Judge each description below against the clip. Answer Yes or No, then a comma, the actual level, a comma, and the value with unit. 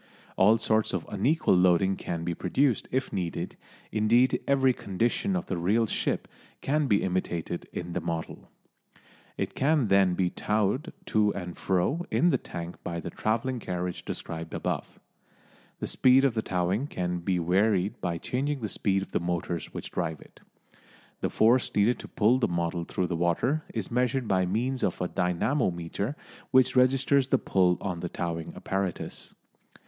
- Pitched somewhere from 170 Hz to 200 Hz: No, low, 100 Hz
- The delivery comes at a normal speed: Yes, average, 165 wpm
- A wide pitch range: Yes, wide, 6.2 semitones